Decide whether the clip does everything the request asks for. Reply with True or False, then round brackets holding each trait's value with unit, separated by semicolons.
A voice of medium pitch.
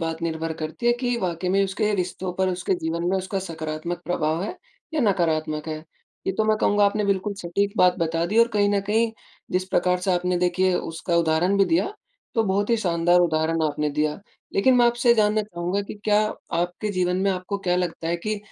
True (180 Hz)